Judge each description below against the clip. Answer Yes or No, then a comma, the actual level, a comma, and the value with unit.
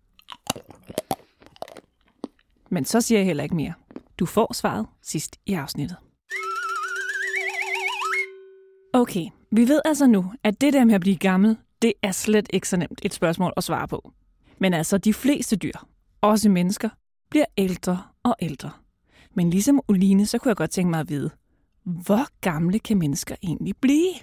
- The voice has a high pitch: Yes, high, 210 Hz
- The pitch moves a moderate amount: No, wide, 5.7 semitones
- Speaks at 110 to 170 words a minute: Yes, average, 160 wpm